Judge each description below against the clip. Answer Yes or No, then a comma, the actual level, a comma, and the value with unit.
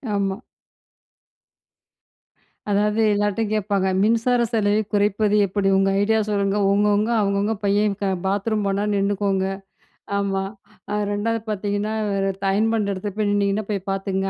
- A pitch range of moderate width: No, narrow, 1.2 semitones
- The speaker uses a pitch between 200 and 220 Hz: Yes, high, 205 Hz